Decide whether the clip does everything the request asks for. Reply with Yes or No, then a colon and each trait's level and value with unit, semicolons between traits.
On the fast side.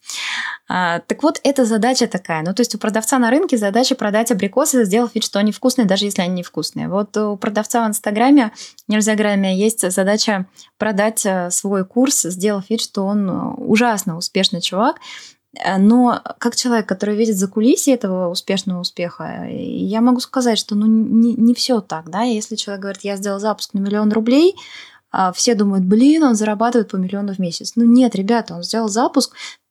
Yes: fast, 180 wpm